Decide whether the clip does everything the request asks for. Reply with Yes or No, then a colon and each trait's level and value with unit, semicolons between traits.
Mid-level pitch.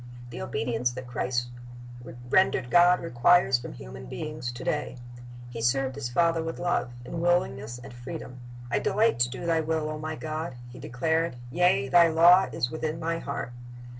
Yes: medium, 150 Hz